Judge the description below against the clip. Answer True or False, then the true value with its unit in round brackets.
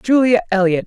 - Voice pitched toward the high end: True (215 Hz)